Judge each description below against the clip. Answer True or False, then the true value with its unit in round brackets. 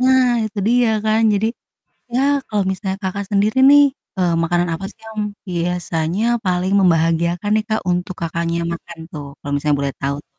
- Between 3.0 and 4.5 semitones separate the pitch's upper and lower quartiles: True (4.1 semitones)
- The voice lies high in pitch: False (180 Hz)